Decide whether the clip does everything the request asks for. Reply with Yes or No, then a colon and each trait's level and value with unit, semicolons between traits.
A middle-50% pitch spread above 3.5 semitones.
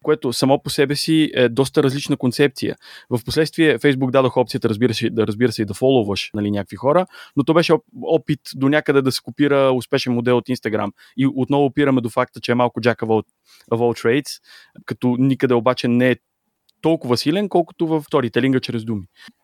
No: average, 3.2 semitones